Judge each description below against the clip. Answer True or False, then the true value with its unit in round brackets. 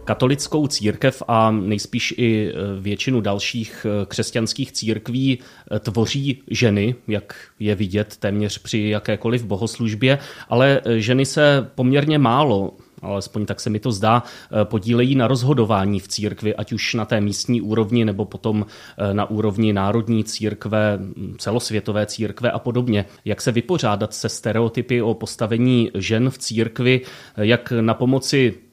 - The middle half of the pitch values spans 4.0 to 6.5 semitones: False (2.7 semitones)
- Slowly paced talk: False (130 wpm)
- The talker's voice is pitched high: False (115 Hz)